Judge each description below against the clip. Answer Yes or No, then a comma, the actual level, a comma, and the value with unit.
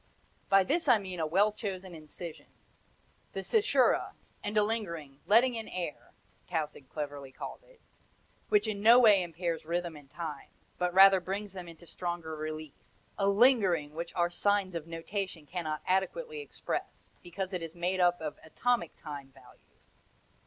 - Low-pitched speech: No, medium, 180 Hz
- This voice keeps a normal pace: Yes, average, 160 wpm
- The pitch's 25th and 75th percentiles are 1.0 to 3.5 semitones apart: No, average, 4.2 semitones